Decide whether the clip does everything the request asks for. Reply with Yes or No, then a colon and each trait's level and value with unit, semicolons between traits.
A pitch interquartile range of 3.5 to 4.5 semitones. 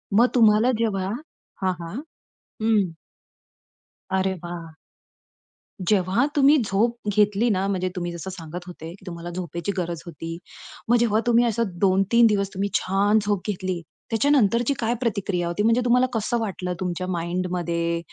Yes: average, 4.1 semitones